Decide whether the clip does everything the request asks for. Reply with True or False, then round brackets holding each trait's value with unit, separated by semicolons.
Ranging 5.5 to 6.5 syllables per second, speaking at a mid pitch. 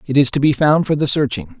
True (6.2 syllables/s; 145 Hz)